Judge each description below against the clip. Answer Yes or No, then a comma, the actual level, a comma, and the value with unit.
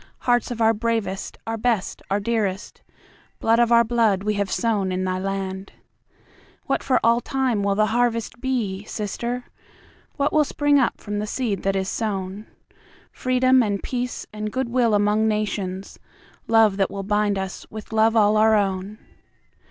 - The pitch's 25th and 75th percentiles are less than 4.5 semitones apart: Yes, average, 2.9 semitones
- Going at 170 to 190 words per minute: No, average, 150 wpm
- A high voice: Yes, high, 215 Hz